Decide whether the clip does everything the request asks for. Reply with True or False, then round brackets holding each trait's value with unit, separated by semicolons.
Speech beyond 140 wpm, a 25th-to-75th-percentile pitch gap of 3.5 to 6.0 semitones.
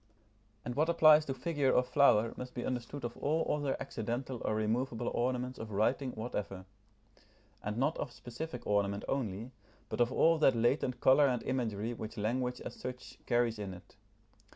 False (170 wpm; 3.1 semitones)